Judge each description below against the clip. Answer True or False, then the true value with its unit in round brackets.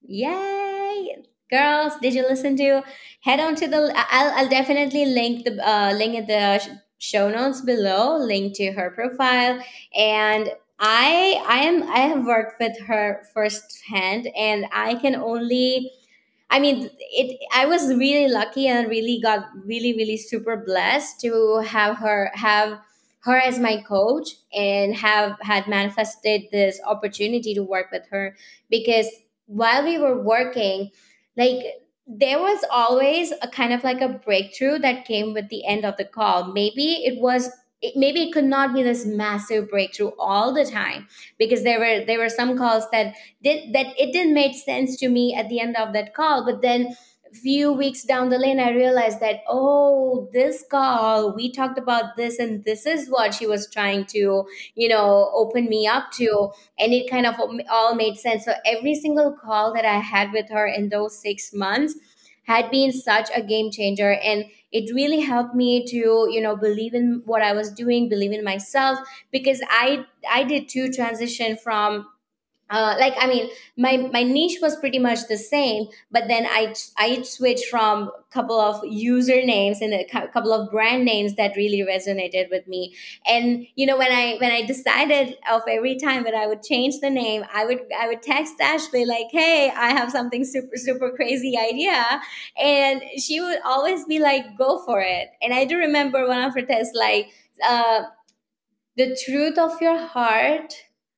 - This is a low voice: False (240 Hz)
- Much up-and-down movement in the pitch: False (3.7 semitones)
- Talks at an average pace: True (180 wpm)